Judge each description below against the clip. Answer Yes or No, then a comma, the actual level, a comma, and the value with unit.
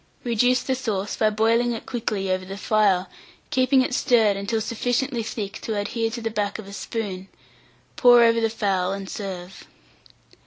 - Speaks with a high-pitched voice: Yes, high, 220 Hz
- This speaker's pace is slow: No, average, 170 wpm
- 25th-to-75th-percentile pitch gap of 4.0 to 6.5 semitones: No, average, 3.0 semitones